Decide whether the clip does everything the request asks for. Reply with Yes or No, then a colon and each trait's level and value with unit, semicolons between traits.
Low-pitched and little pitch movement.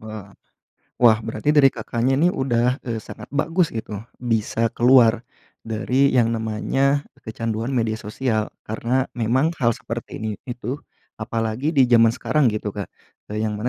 No: low, 115 Hz; average, 3.1 semitones